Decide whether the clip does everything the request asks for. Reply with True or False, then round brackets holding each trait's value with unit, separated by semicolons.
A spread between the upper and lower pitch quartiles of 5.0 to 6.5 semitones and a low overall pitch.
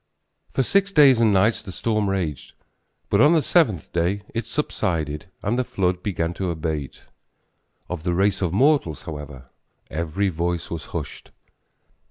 True (5.5 semitones; 95 Hz)